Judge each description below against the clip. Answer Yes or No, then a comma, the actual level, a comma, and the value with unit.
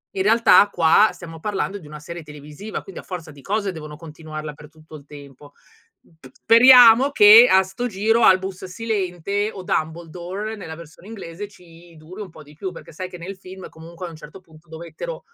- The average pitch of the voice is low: No, medium, 180 Hz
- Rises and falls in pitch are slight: No, average, 4.3 semitones